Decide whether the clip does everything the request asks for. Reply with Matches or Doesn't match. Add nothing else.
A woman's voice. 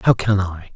Doesn't match